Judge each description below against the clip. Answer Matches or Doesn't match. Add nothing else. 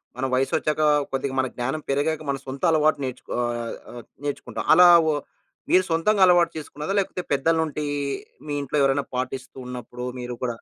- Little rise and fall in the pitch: Doesn't match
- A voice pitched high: Doesn't match